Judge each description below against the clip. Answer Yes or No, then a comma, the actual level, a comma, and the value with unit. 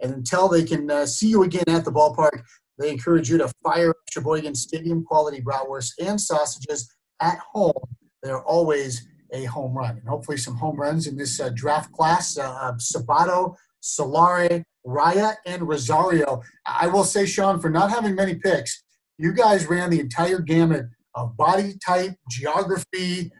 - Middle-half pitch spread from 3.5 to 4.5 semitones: Yes, average, 4.0 semitones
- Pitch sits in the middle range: Yes, medium, 160 Hz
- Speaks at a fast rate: No, average, 160 wpm